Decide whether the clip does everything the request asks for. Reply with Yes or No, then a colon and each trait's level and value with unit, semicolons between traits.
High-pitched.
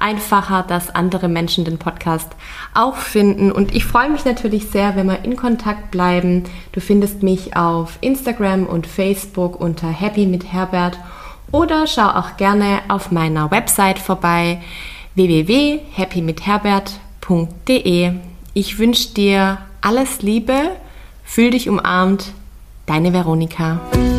Yes: high, 195 Hz